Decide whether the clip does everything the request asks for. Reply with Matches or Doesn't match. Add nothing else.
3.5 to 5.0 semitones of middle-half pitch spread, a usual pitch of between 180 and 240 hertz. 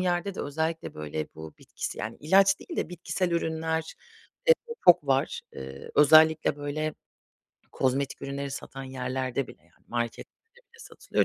Doesn't match